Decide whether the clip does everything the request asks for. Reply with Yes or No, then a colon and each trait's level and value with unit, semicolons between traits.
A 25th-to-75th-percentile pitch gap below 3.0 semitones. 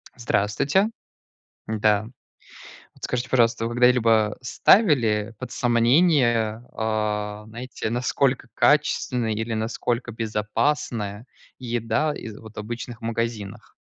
Yes: narrow, 2.5 semitones